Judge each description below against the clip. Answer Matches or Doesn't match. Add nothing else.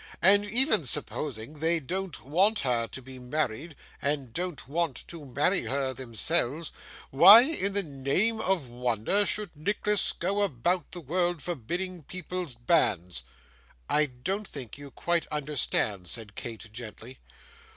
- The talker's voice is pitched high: Doesn't match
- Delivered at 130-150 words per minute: Matches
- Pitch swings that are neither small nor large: Doesn't match